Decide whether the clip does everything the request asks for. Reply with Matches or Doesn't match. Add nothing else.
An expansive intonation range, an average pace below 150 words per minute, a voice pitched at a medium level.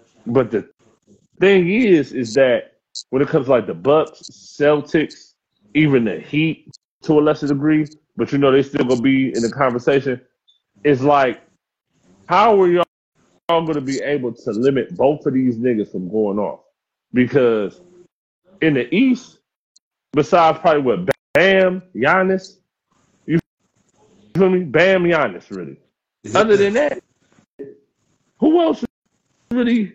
Matches